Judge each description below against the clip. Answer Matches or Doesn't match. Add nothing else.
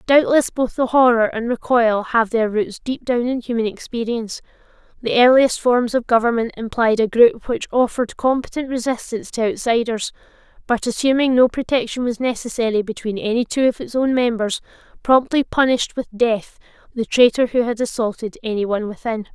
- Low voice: Doesn't match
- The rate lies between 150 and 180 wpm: Matches